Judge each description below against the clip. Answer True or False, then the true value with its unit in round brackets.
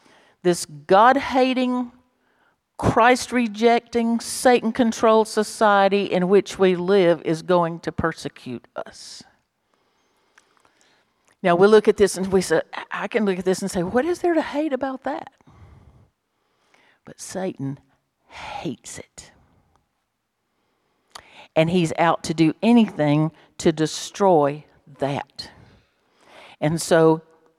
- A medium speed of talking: False (115 wpm)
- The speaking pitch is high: True (195 Hz)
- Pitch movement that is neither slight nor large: False (6.0 semitones)